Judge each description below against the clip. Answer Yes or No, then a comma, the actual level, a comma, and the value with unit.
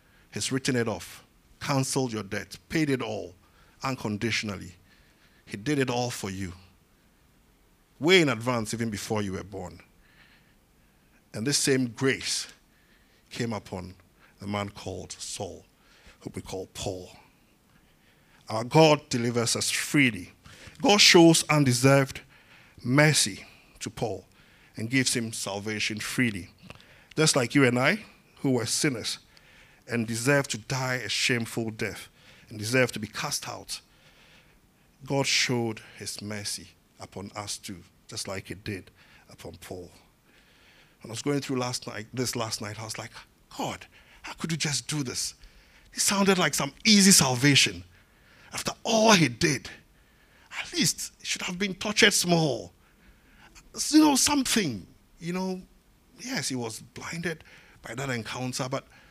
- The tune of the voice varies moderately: No, wide, 5.8 semitones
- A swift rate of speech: No, average, 145 wpm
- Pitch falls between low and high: No, low, 120 Hz